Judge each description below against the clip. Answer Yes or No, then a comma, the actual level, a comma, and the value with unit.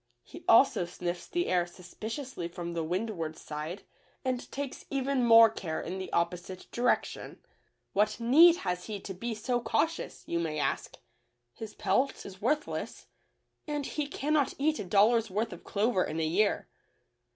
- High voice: Yes, high, 215 Hz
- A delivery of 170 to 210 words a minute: No, average, 160 wpm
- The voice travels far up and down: Yes, wide, 6.4 semitones